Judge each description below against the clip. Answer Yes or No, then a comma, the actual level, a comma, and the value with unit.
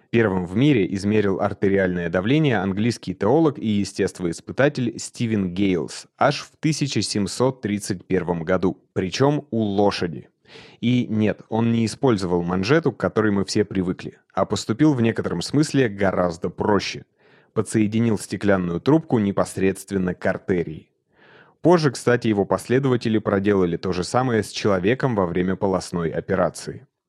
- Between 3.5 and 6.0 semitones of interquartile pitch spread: Yes, average, 4.0 semitones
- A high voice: No, low, 105 Hz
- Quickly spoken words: No, average, 130 wpm